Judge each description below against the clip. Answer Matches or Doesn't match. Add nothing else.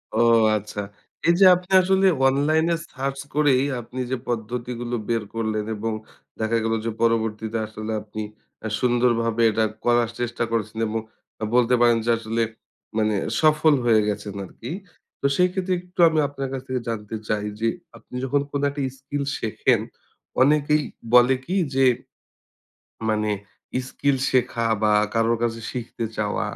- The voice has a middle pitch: Doesn't match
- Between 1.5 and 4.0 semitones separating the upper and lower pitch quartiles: Matches